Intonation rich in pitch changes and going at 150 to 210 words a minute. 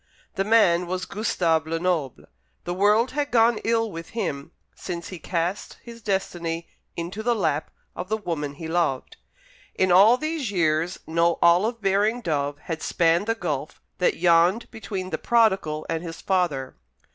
No: average, 4.6 semitones; average, 160 wpm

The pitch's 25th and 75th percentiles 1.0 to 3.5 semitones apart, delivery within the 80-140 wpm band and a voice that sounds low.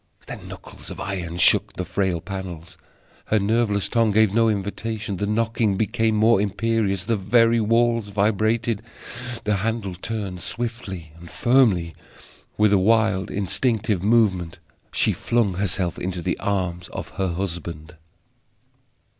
Yes: average, 3.2 semitones; slow, 135 wpm; low, 100 Hz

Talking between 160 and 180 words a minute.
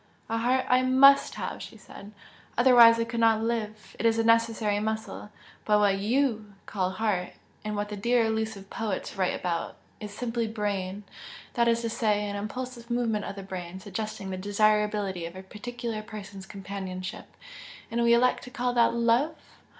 Yes: average, 175 wpm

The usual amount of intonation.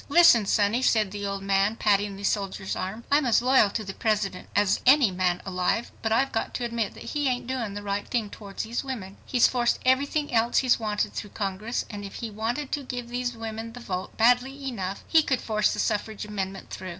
Yes: average, 3.6 semitones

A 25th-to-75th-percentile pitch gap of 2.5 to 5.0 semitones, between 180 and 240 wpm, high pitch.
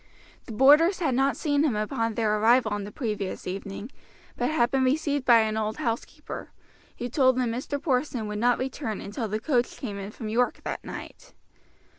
Yes: average, 3.9 semitones; average, 190 wpm; high, 240 Hz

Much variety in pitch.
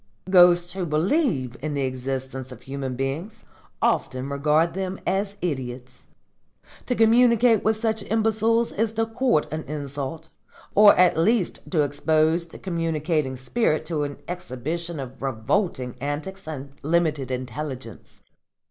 Yes: wide, 6.3 semitones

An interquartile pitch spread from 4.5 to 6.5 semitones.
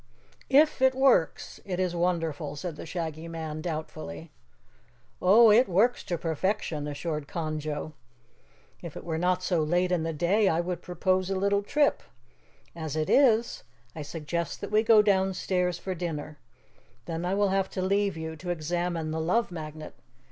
No: average, 3.3 semitones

